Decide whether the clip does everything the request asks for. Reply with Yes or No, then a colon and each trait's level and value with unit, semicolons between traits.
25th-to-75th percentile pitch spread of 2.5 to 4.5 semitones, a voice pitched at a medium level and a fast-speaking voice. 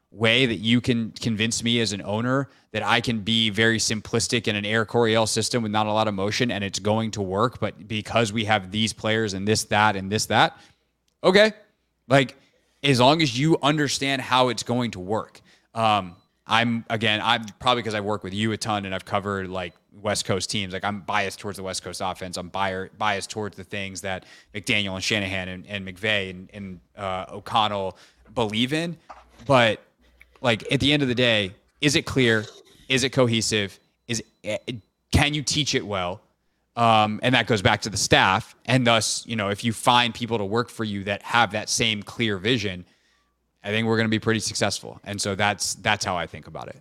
No: average, 2.9 semitones; low, 110 Hz; fast, 210 wpm